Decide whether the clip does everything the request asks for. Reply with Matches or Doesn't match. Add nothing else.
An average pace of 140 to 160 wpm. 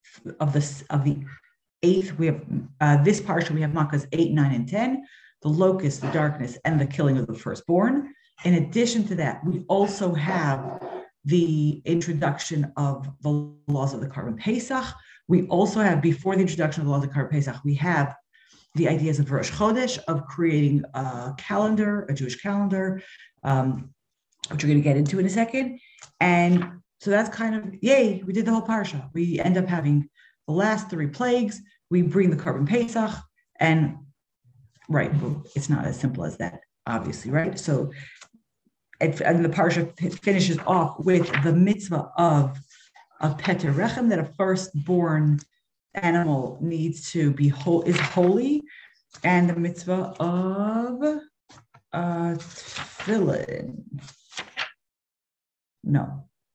Matches